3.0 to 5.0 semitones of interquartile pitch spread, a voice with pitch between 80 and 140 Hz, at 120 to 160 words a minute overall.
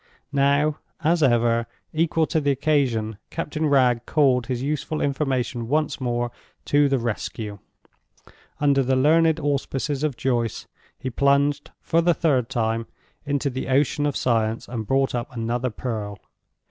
Yes: average, 3.5 semitones; low, 135 Hz; average, 145 wpm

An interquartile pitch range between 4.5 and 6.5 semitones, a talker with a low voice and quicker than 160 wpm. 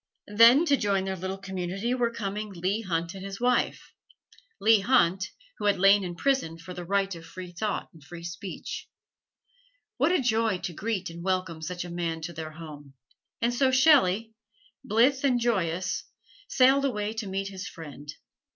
No: average, 4.8 semitones; high, 195 Hz; average, 175 wpm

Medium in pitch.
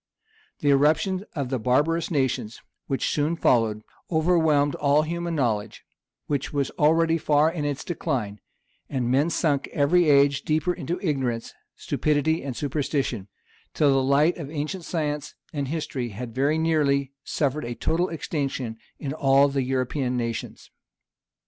Yes: medium, 145 Hz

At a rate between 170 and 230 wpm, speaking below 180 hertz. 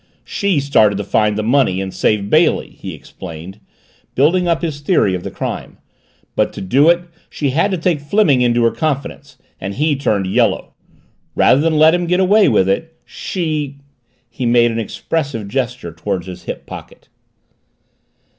Yes: average, 175 wpm; low, 135 Hz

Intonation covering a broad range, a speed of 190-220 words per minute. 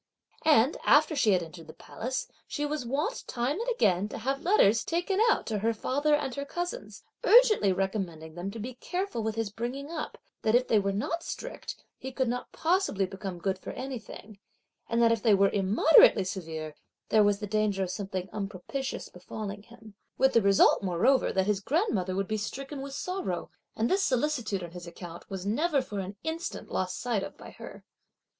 Yes: wide, 6.2 semitones; average, 195 wpm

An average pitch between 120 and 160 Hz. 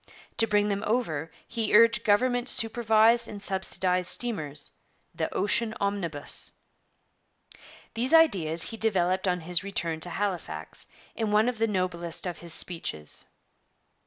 No: high, 200 Hz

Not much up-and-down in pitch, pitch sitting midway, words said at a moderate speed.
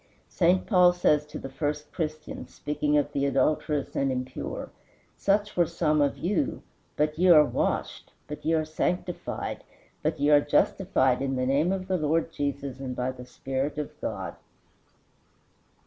No: average, 3.3 semitones; medium, 150 Hz; average, 165 wpm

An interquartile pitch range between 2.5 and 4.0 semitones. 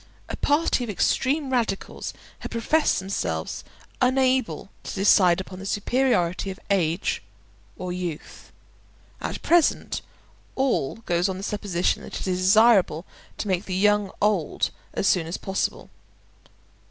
No: average, 4.7 semitones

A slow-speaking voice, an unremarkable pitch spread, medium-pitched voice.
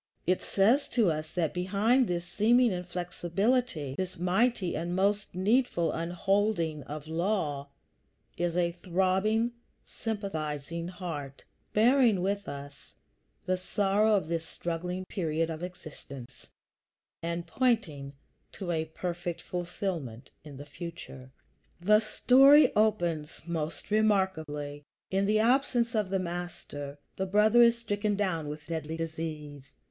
Yes: slow, 120 wpm; average, 4.5 semitones; medium, 180 Hz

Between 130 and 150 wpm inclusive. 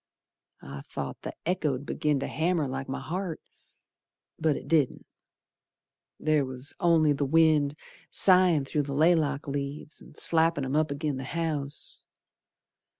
Yes: average, 140 wpm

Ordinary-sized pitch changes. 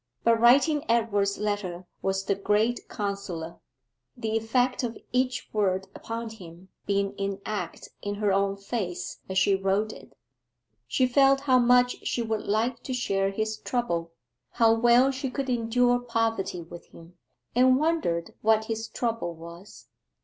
Yes: average, 3.9 semitones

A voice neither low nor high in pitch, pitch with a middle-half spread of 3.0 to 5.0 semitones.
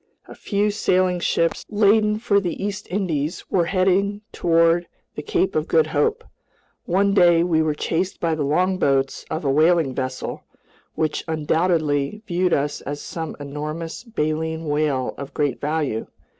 Yes: medium, 165 Hz; average, 4.3 semitones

